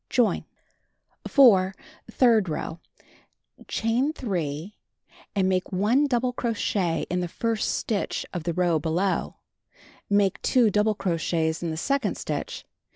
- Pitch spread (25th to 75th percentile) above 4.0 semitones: Yes, average, 4.9 semitones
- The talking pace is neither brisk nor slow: No, slow, 130 wpm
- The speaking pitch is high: Yes, high, 195 Hz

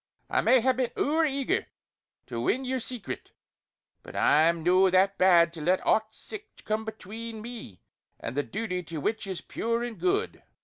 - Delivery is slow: No, average, 175 wpm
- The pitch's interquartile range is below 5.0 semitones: No, wide, 5.5 semitones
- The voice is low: No, high, 220 Hz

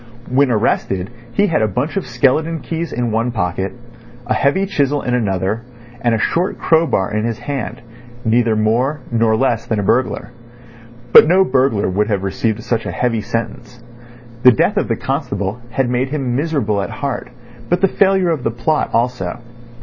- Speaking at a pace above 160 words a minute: Yes, average, 180 wpm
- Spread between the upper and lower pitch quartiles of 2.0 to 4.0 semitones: No, average, 4.5 semitones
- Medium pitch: No, low, 120 Hz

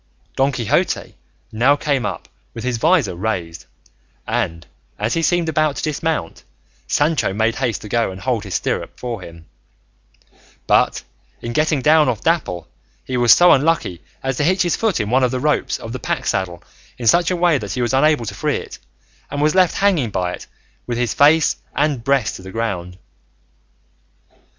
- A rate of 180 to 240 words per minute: Yes, average, 185 wpm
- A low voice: Yes, low, 125 Hz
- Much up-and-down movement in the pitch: Yes, wide, 6.0 semitones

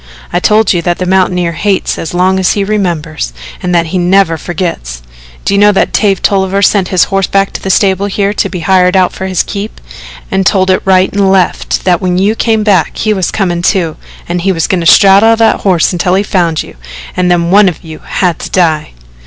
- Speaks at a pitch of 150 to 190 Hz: Yes, medium, 185 Hz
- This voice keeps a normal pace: No, fast, 225 wpm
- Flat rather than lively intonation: Yes, narrow, 2.2 semitones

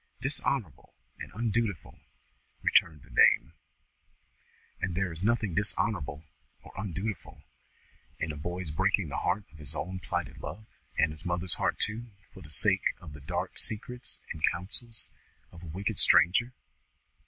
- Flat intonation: No, average, 5.3 semitones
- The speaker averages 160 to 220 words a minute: No, average, 145 wpm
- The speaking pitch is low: Yes, very low, 90 Hz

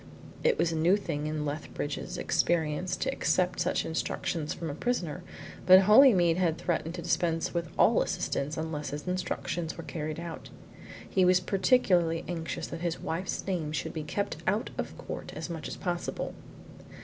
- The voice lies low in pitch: No, medium, 170 Hz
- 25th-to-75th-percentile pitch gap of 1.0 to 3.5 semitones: Yes, narrow, 2.6 semitones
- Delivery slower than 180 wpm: Yes, average, 170 wpm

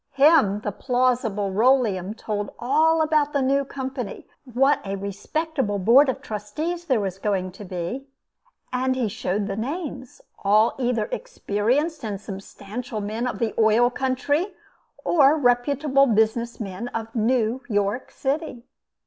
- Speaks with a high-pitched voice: Yes, high, 245 Hz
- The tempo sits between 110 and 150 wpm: Yes, average, 140 wpm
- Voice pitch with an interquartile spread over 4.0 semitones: Yes, average, 4.9 semitones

